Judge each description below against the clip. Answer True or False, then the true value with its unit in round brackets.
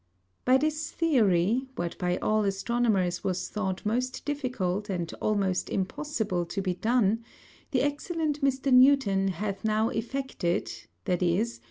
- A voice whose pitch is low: False (215 Hz)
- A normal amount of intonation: False (5.8 semitones)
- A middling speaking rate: False (130 wpm)